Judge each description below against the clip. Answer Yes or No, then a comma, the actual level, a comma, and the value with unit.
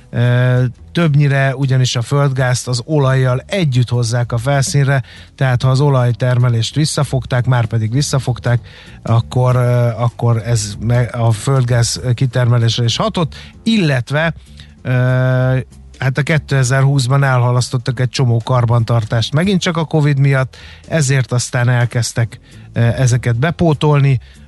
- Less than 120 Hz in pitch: No, low, 125 Hz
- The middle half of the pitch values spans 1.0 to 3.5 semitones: Yes, narrow, 2.5 semitones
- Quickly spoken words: No, average, 110 wpm